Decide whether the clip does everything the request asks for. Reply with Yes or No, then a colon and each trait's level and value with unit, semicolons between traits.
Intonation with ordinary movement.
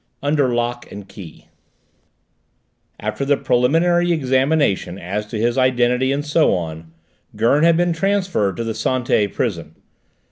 No: wide, 6.1 semitones